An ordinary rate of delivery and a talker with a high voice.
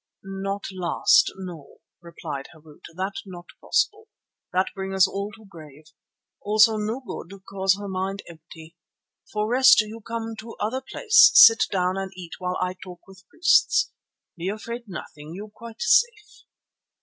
Yes: average, 150 wpm; high, 195 Hz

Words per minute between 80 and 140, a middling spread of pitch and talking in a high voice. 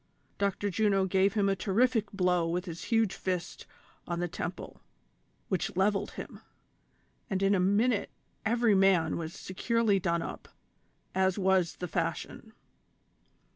No: slow, 135 wpm; narrow, 2.3 semitones; high, 195 Hz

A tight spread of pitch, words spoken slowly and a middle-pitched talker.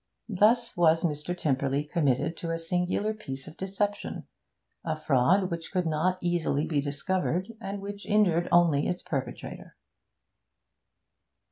No: average, 4.0 semitones; slow, 130 wpm; medium, 170 Hz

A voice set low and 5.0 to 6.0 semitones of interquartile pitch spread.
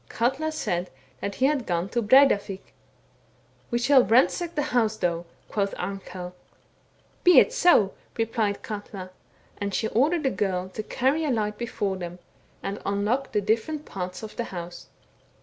No: high, 215 Hz; wide, 5.5 semitones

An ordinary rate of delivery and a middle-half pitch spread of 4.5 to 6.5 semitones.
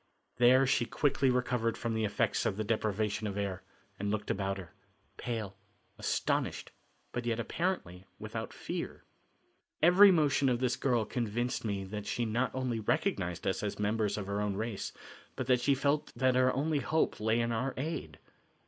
No: average, 175 wpm; average, 3.9 semitones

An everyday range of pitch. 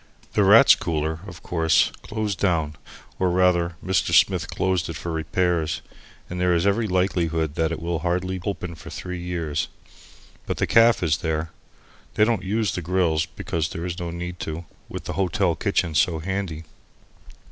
No: narrow, 2.3 semitones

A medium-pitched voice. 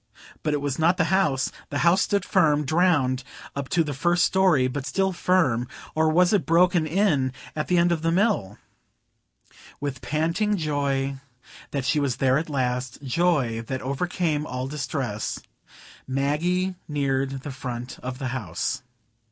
Yes: medium, 145 Hz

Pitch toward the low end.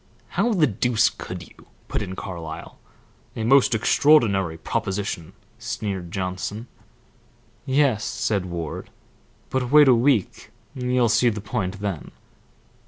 Yes: low, 105 Hz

